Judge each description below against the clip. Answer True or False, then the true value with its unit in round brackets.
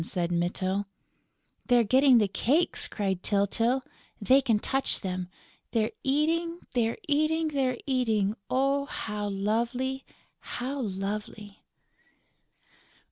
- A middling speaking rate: False (105 wpm)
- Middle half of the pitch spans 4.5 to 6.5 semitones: True (5.0 semitones)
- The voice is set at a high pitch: True (235 Hz)